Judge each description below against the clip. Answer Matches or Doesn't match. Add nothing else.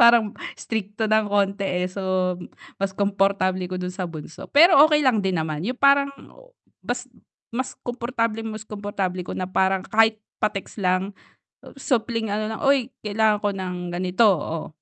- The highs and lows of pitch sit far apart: Doesn't match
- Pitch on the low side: Doesn't match